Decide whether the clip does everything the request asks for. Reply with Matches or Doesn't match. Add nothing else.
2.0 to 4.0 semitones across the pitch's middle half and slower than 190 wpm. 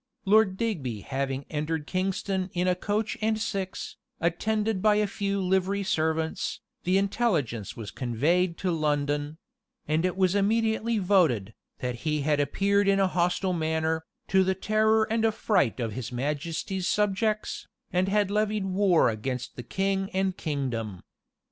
Doesn't match